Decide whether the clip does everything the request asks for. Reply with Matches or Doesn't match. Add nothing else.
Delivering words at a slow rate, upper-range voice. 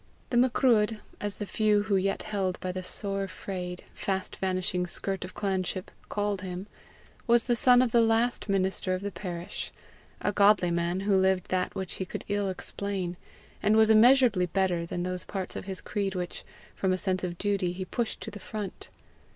Doesn't match